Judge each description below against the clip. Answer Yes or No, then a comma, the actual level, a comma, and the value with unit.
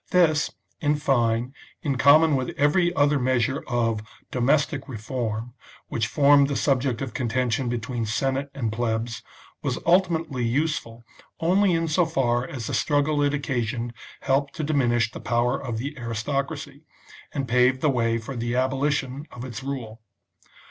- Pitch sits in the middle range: No, low, 130 Hz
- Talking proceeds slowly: No, average, 155 wpm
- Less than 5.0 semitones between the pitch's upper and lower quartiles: Yes, average, 3.5 semitones